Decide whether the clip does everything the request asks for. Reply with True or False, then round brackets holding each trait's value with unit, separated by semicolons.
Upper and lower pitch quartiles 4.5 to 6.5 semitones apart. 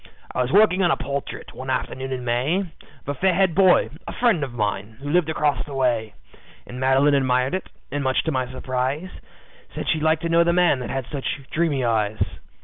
True (4.8 semitones)